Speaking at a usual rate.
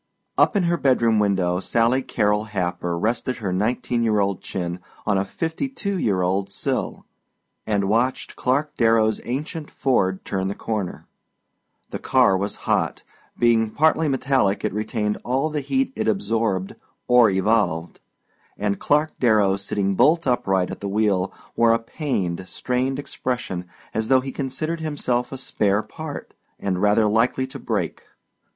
Yes: average, 155 wpm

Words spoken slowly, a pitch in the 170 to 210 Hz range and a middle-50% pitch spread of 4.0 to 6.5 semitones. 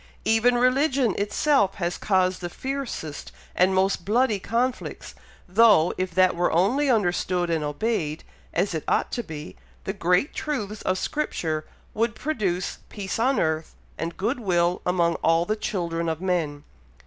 No: average, 150 wpm; high, 190 Hz; average, 5.1 semitones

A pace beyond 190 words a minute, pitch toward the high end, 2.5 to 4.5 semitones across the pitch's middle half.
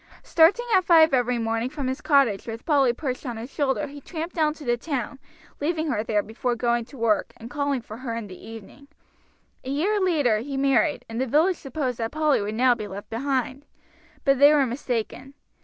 Yes: fast, 205 wpm; very high, 265 Hz; average, 4.2 semitones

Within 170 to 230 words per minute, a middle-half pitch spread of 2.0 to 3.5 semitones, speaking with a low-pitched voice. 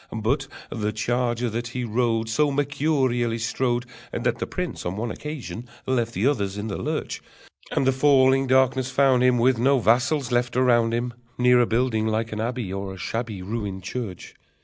Yes: average, 180 wpm; narrow, 2.6 semitones; low, 120 Hz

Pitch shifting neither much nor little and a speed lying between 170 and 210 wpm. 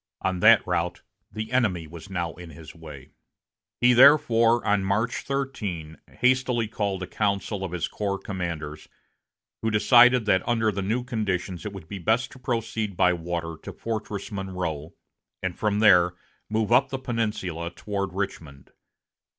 No: average, 4.4 semitones; average, 155 wpm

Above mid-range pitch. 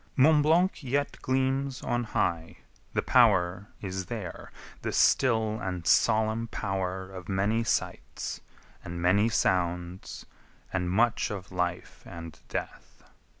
No: low, 100 Hz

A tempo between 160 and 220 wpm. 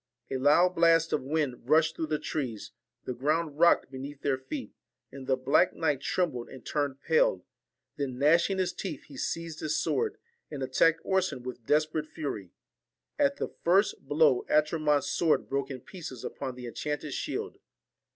Yes: average, 165 wpm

